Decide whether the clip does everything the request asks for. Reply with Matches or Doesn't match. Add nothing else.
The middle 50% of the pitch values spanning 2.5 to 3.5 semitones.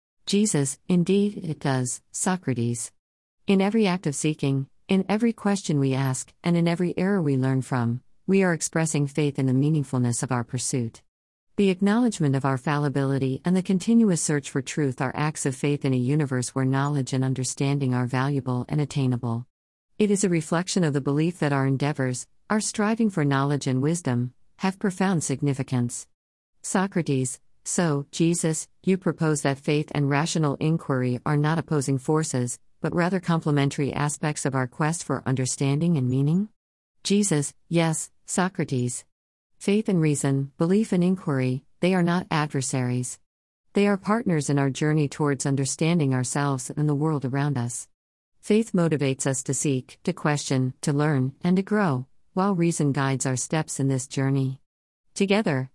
Doesn't match